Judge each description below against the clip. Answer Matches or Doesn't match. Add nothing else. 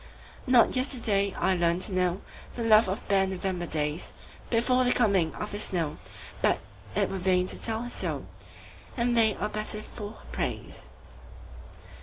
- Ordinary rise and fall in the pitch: Matches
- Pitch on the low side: Doesn't match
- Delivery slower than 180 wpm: Matches